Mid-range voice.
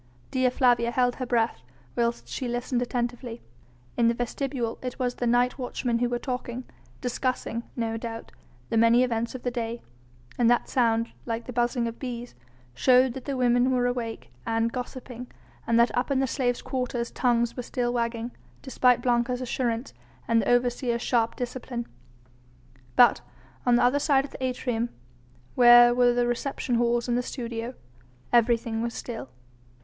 No: high, 240 Hz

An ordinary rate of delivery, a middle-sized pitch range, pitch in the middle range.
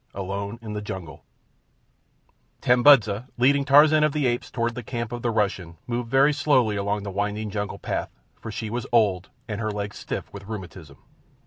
No: average, 180 wpm; average, 3.4 semitones; low, 110 Hz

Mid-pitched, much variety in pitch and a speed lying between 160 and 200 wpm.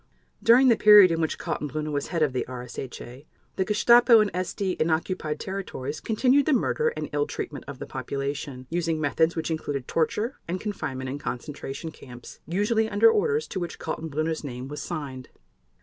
Yes: medium, 160 Hz; wide, 6.7 semitones; average, 175 wpm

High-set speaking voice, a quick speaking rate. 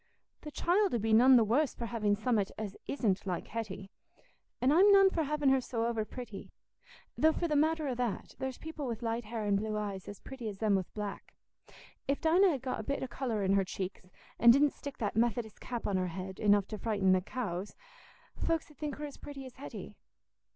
Yes: high, 235 Hz; fast, 220 wpm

